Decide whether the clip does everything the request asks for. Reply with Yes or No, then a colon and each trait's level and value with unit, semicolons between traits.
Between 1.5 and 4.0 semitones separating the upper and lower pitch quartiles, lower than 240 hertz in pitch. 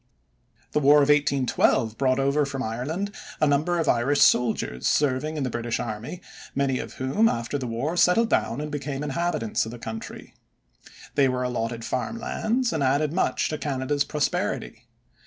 Yes: average, 3.5 semitones; medium, 140 Hz